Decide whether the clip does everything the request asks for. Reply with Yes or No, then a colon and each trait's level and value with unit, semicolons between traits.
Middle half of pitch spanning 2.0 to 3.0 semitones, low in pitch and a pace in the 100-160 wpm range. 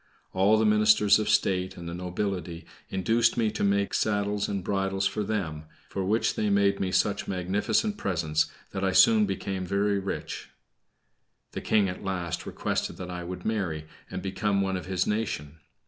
No: narrow, 2.4 semitones; very low, 95 Hz; average, 175 wpm